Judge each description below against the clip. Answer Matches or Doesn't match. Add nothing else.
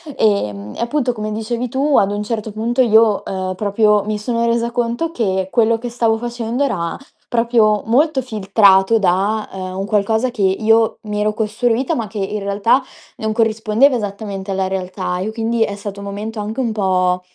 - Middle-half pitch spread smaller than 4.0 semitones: Matches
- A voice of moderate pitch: Doesn't match